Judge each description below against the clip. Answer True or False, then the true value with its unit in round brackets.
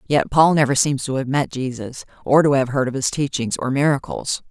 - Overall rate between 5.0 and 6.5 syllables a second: True (5.4 syllables/s)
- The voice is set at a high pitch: False (135 Hz)